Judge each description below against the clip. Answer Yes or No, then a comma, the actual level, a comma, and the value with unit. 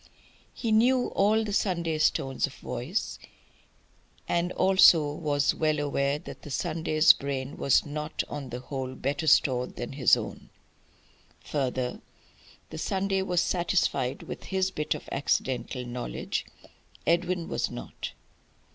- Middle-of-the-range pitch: Yes, medium, 150 Hz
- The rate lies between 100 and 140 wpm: Yes, slow, 135 wpm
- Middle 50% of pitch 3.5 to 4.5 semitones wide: No, average, 5.1 semitones